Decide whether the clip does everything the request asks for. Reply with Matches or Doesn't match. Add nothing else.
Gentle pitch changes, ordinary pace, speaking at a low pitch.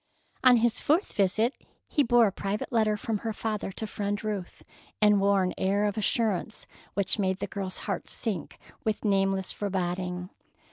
Doesn't match